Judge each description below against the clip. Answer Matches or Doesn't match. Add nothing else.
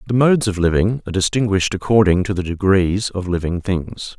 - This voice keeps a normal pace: Matches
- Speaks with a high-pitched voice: Doesn't match